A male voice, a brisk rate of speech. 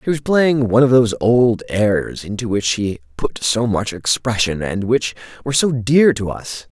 No: male; average, 195 wpm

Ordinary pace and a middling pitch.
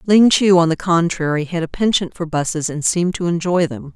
No: fast, 225 wpm; medium, 170 Hz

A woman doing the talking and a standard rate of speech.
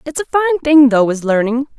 No: female; fast, 235 wpm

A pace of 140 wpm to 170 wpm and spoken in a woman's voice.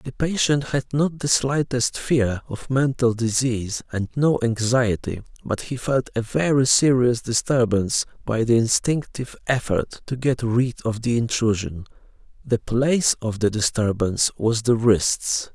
No: average, 145 wpm; male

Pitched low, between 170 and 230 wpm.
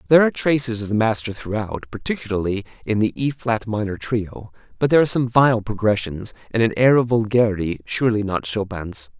Yes: low, 110 Hz; average, 185 wpm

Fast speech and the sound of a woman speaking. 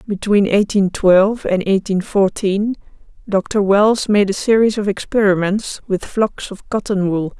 No: average, 145 wpm; female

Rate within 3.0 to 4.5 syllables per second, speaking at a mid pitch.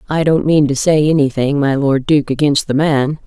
No: 5.0 syllables/s; medium, 145 Hz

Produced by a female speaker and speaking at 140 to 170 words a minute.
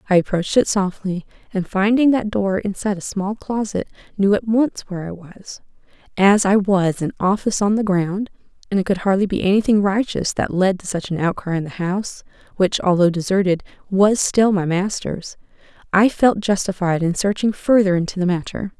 No: female; average, 190 wpm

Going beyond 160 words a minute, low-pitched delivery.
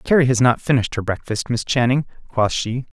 Yes: average, 200 wpm; low, 125 Hz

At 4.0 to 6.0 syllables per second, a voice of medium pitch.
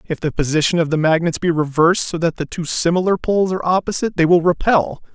No: 6.5 syllables/s; medium, 170 Hz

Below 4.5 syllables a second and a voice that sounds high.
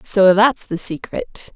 Yes: 3.5 syllables/s; high, 220 Hz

